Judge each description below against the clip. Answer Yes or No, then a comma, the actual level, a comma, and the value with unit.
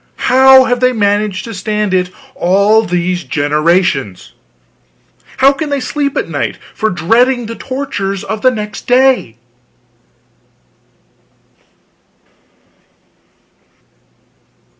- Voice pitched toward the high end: Yes, high, 215 Hz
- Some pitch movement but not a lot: No, wide, 5.8 semitones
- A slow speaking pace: Yes, slow, 95 wpm